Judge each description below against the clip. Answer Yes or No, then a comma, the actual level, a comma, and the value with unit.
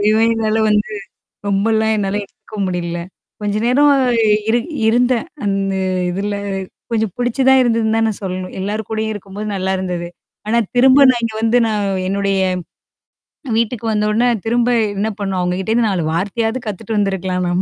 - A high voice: Yes, high, 210 Hz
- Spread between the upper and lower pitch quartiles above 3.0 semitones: No, average, 2.7 semitones